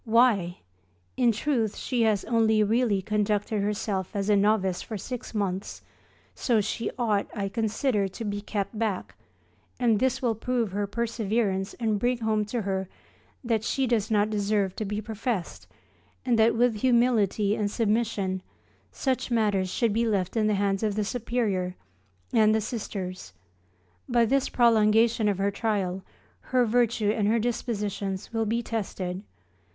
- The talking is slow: No, average, 155 wpm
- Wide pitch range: No, narrow, 2.6 semitones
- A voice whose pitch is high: Yes, high, 215 Hz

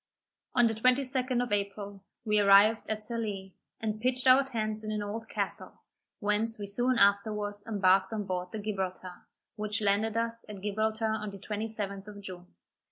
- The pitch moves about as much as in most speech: No, narrow, 1.9 semitones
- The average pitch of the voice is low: No, high, 210 Hz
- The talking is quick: No, average, 165 wpm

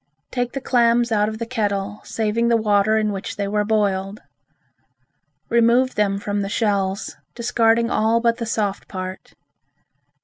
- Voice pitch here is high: Yes, high, 215 Hz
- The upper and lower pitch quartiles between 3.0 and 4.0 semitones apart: No, narrow, 2.5 semitones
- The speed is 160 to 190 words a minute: No, average, 150 wpm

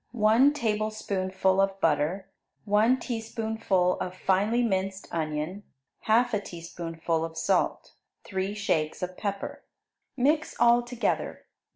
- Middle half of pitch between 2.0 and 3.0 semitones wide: No, average, 3.7 semitones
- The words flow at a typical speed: No, slow, 105 wpm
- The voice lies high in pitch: Yes, high, 200 Hz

